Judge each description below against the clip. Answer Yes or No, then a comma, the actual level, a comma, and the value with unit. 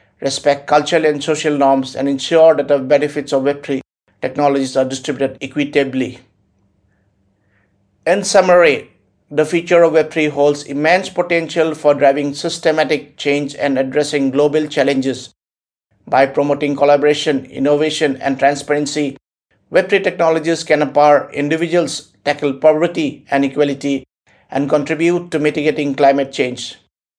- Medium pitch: Yes, medium, 145 Hz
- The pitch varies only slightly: Yes, narrow, 2.1 semitones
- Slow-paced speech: Yes, slow, 120 wpm